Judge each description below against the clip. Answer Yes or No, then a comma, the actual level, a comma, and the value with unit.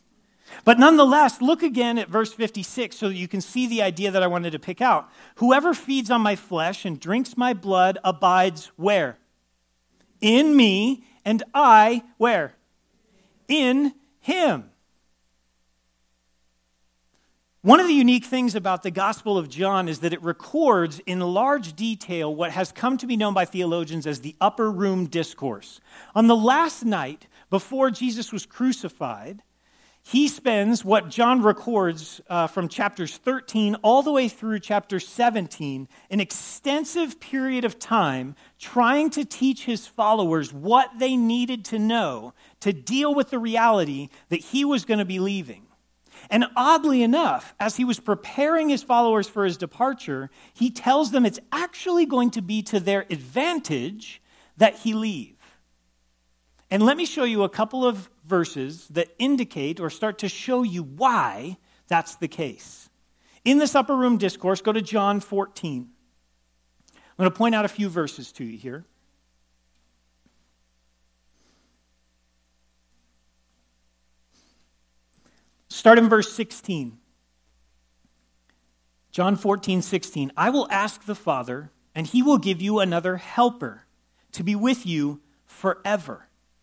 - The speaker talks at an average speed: Yes, average, 145 wpm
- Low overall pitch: No, high, 200 Hz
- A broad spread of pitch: Yes, wide, 8.7 semitones